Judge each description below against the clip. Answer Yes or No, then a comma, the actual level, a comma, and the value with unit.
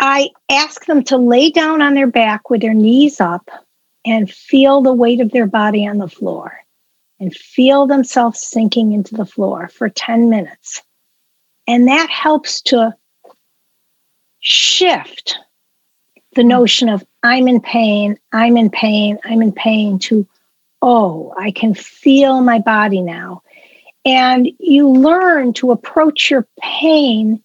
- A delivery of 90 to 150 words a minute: Yes, average, 140 wpm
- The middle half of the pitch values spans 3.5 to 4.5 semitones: Yes, average, 4.2 semitones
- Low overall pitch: No, high, 240 Hz